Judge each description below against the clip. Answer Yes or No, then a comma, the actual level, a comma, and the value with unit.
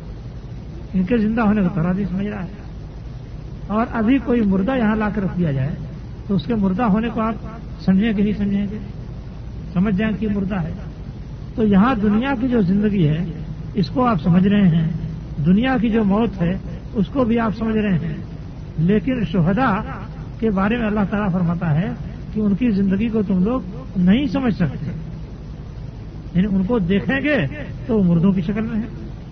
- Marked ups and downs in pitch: No, average, 4.6 semitones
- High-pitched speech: Yes, high, 195 Hz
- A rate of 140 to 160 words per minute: No, average, 185 wpm